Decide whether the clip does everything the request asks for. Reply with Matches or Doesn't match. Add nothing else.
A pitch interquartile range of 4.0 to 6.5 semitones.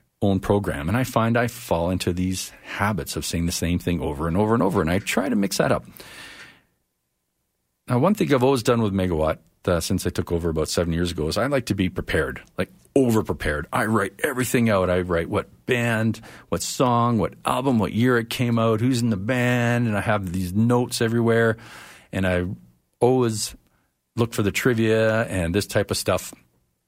Matches